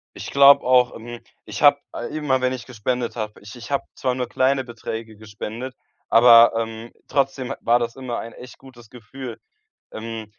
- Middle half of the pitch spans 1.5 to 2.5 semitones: Yes, narrow, 2.2 semitones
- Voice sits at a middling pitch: No, low, 120 Hz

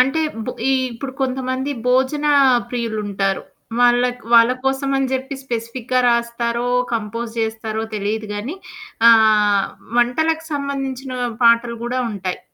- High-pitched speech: Yes, high, 240 Hz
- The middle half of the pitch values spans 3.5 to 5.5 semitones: No, average, 2.9 semitones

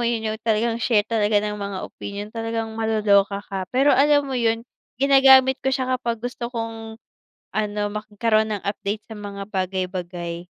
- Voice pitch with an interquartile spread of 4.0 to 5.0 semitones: No, average, 2.7 semitones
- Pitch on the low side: No, high, 220 Hz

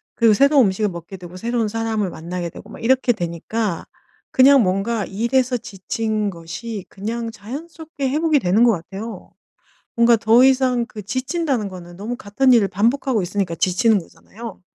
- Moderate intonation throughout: Yes, average, 4.3 semitones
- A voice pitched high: Yes, high, 225 Hz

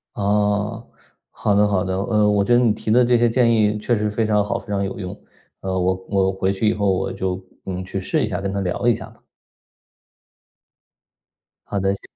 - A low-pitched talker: Yes, low, 100 Hz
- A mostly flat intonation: Yes, narrow, 1.9 semitones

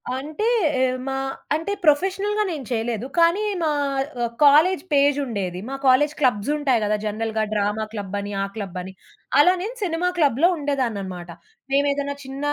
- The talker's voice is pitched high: Yes, very high, 275 Hz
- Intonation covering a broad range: Yes, wide, 6.0 semitones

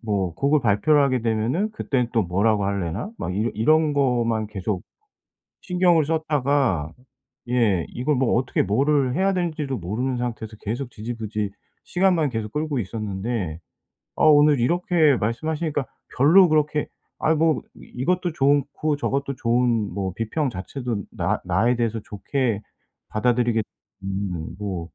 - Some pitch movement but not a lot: No, wide, 5.8 semitones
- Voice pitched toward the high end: No, low, 125 Hz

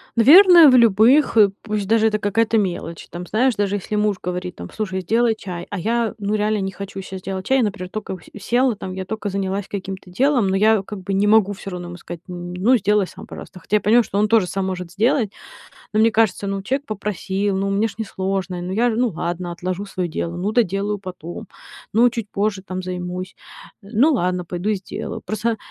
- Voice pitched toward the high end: Yes, high, 200 Hz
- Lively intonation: No, average, 3.0 semitones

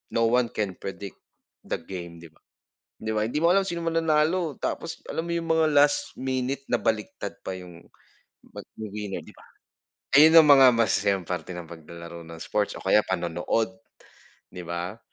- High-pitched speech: No, low, 110 Hz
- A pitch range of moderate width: No, wide, 8.8 semitones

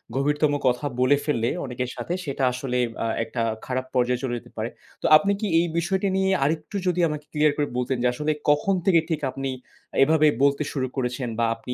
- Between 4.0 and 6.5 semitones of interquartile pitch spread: No, average, 3.6 semitones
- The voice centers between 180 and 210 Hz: No, medium, 140 Hz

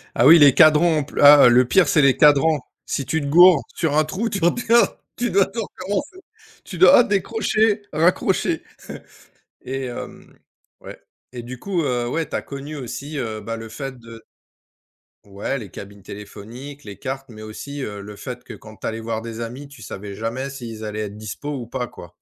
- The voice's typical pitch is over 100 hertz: Yes, low, 135 Hz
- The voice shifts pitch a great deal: Yes, wide, 5.9 semitones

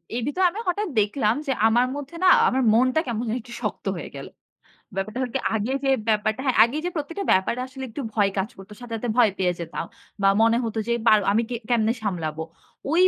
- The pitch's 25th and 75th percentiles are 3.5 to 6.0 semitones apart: Yes, average, 4.0 semitones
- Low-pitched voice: No, high, 235 Hz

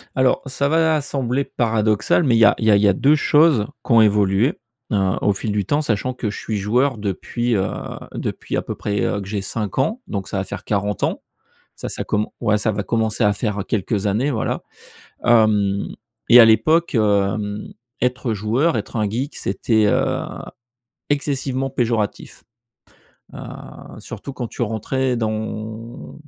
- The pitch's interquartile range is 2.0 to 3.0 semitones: No, average, 3.9 semitones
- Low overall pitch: Yes, low, 110 Hz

